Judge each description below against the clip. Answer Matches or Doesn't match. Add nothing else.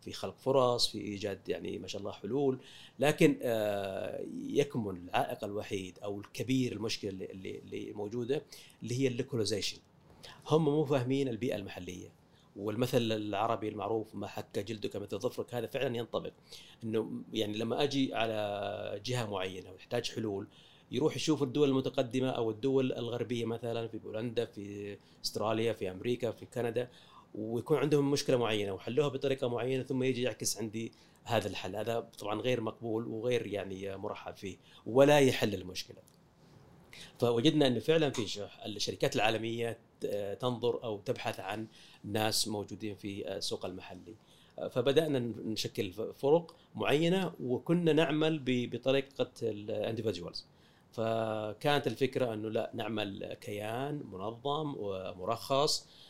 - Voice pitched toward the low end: Matches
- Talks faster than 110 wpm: Matches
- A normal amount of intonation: Matches